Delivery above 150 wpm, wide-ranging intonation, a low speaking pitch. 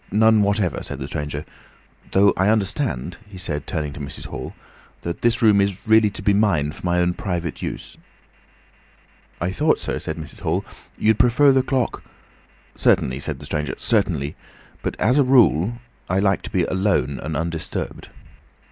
Yes: average, 165 wpm; wide, 5.8 semitones; very low, 95 Hz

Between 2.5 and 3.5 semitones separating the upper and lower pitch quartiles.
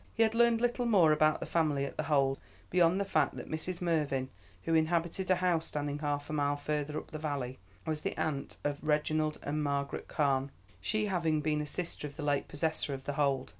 Yes: average, 2.9 semitones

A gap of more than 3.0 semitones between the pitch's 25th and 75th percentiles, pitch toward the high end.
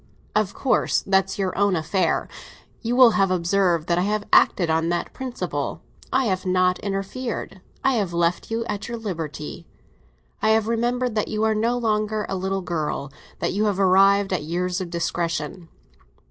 Yes: average, 3.7 semitones; high, 195 Hz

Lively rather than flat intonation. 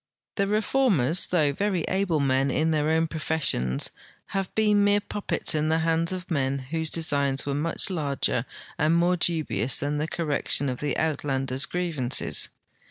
No: average, 4.1 semitones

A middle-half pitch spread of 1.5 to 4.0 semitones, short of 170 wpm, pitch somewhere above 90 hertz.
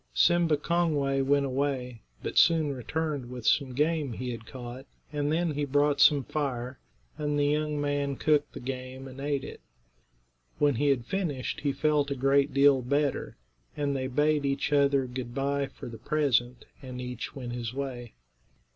No: narrow, 2.4 semitones; average, 175 wpm; medium, 140 Hz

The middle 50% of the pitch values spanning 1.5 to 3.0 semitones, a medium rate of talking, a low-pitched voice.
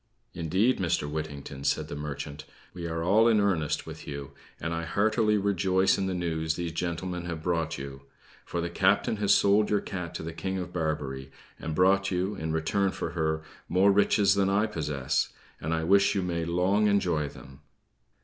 No: average, 3.8 semitones; average, 190 wpm; very low, 85 Hz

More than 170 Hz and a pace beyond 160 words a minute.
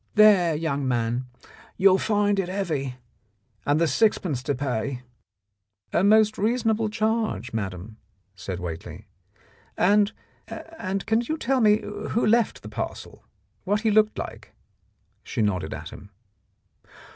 No: medium, 185 Hz; average, 140 wpm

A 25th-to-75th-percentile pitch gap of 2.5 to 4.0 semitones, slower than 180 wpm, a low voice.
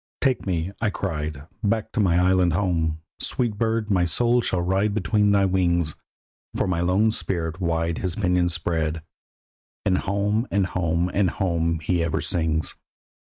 Yes: average, 3.4 semitones; average, 155 wpm; very low, 90 Hz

